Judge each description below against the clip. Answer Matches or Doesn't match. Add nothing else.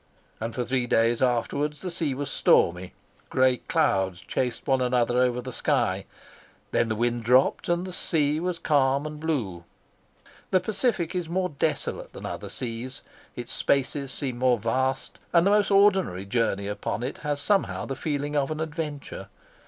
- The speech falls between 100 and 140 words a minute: Doesn't match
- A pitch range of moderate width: Matches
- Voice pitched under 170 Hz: Matches